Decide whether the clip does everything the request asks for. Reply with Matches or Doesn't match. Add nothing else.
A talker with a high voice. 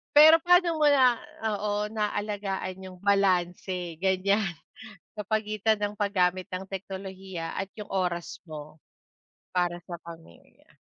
Matches